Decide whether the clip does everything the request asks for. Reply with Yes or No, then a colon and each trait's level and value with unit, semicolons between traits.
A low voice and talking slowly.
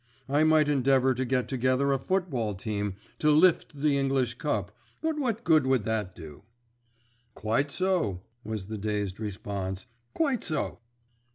No: low, 130 Hz; average, 150 wpm